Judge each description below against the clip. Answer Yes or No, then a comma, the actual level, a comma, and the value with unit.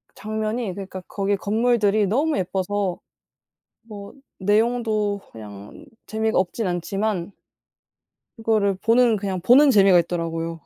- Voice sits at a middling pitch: No, high, 205 Hz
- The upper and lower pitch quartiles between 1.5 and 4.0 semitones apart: Yes, average, 2.9 semitones